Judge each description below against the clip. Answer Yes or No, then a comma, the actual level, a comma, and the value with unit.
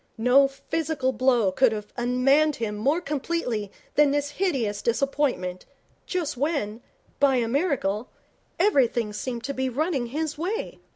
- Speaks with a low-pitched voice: No, very high, 265 Hz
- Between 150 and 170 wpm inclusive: No, slow, 135 wpm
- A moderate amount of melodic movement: Yes, average, 4.2 semitones